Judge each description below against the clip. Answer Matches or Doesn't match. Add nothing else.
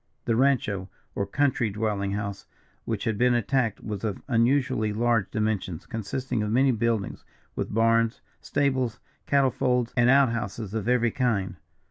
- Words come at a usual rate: Matches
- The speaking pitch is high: Doesn't match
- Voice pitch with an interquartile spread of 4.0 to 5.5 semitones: Doesn't match